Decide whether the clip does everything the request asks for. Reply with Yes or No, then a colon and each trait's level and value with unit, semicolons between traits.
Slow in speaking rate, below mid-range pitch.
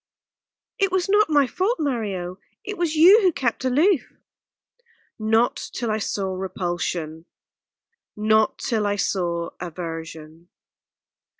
No: slow, 115 wpm; high, 215 Hz